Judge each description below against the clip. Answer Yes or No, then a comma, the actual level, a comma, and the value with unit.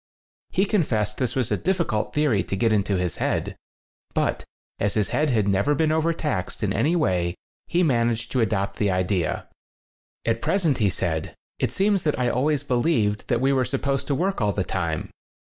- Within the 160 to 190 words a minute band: No, average, 200 wpm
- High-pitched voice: No, low, 120 Hz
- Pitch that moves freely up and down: Yes, wide, 7.0 semitones